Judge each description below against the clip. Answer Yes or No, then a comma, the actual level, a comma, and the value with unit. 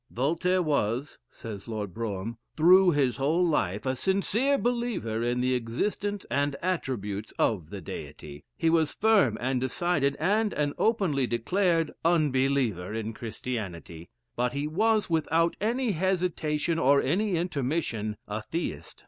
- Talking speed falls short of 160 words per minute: Yes, average, 140 wpm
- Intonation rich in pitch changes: Yes, wide, 7.7 semitones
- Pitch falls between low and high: Yes, medium, 145 Hz